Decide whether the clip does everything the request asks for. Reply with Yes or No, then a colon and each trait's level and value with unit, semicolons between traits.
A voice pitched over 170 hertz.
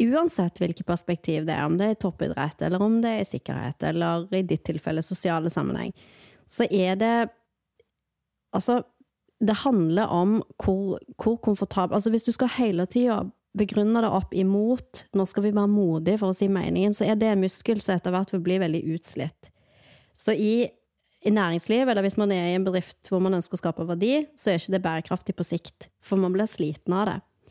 Yes: high, 190 Hz